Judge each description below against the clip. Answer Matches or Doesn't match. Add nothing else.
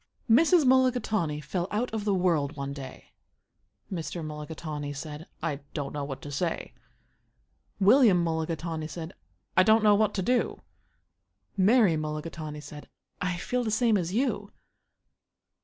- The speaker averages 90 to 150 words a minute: Matches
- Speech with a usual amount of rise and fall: Doesn't match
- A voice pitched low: Doesn't match